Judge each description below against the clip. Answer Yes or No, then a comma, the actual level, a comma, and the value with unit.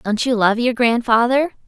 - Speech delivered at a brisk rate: No, average, 180 wpm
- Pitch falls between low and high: No, high, 235 Hz